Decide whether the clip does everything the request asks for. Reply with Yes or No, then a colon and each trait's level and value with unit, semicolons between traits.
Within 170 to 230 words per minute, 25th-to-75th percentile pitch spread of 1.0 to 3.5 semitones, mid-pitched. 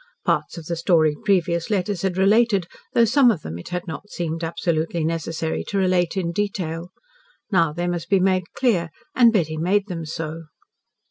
Yes: average, 180 wpm; average, 3.0 semitones; medium, 175 Hz